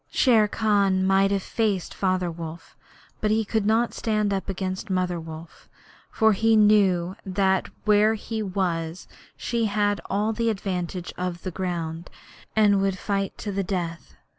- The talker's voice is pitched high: Yes, high, 195 Hz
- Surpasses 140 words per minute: Yes, average, 155 wpm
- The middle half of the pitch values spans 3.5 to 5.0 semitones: No, average, 2.7 semitones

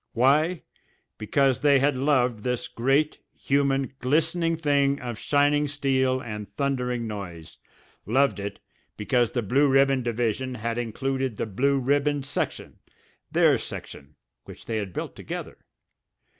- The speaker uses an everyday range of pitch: Yes, average, 3.3 semitones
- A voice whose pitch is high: No, low, 130 Hz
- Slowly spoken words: Yes, slow, 130 wpm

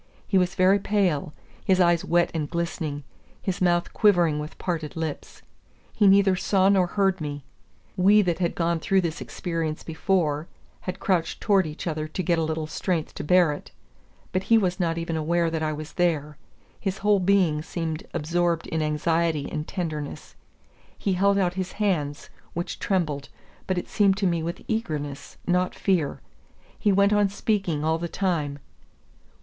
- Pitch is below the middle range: No, medium, 175 Hz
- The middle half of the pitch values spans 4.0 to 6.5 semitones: No, average, 3.4 semitones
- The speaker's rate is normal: Yes, average, 170 wpm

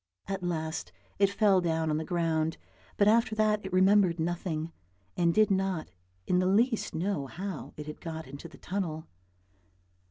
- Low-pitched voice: No, medium, 175 Hz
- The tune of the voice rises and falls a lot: No, average, 3.7 semitones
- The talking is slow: No, average, 165 wpm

